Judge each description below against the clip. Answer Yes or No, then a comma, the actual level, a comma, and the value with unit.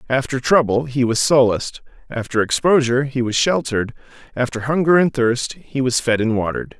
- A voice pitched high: No, low, 130 Hz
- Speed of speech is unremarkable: Yes, average, 170 wpm